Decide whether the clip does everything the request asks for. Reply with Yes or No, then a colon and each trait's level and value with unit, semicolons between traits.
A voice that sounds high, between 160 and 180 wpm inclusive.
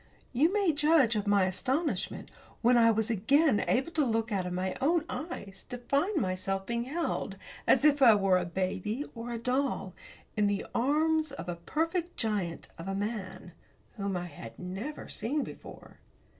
Yes: high, 230 Hz; average, 175 wpm